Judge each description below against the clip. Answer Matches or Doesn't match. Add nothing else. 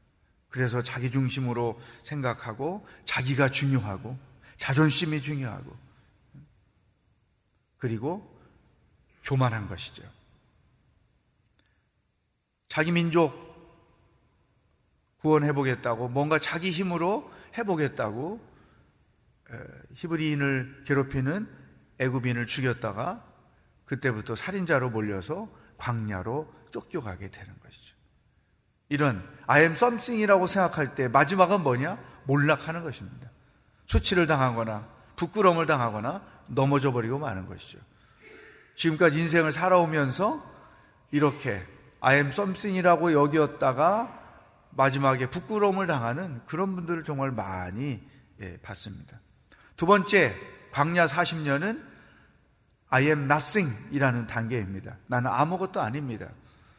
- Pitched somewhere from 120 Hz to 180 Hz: Matches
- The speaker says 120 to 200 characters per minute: Doesn't match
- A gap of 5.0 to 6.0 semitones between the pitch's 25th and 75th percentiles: Matches